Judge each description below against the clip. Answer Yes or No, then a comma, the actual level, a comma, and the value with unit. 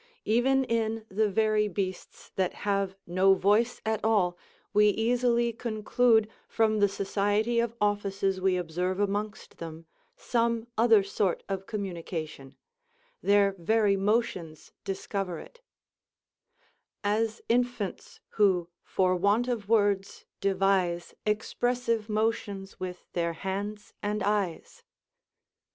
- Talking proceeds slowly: Yes, slow, 110 wpm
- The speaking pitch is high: Yes, high, 205 Hz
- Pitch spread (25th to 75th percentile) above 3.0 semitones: No, average, 2.7 semitones